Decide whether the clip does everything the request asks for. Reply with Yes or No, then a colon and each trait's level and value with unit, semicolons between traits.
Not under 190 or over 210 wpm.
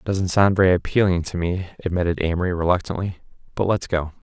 No: average, 165 wpm